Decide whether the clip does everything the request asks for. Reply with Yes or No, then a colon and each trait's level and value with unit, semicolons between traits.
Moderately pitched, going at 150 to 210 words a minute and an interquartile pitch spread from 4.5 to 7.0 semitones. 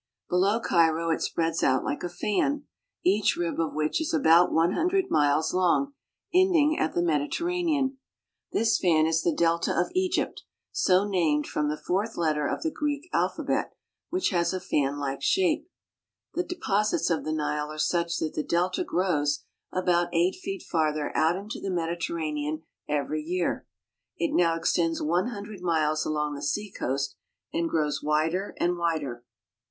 Yes: medium, 170 Hz; average, 160 wpm; average, 5.1 semitones